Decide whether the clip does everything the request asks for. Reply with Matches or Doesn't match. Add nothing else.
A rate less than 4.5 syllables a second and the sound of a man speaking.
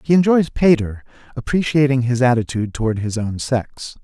Doesn't match